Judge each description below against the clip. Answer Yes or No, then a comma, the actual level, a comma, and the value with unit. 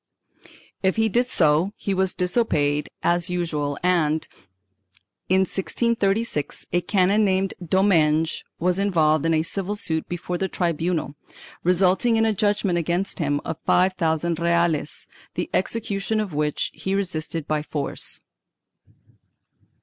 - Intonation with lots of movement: No, average, 3.6 semitones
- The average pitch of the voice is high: No, medium, 180 Hz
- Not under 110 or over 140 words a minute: Yes, slow, 135 wpm